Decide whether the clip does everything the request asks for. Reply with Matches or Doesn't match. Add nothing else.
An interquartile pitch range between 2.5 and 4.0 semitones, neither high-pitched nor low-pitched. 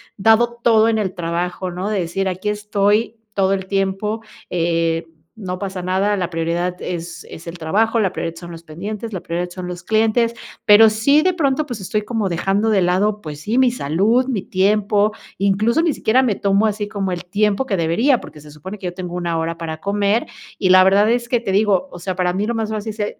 Doesn't match